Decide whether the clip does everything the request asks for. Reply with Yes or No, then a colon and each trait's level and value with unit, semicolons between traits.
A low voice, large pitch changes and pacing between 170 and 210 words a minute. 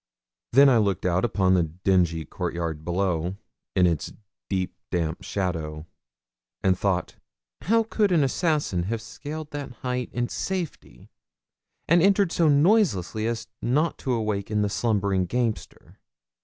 No: low, 105 Hz; wide, 8.0 semitones; slow, 135 wpm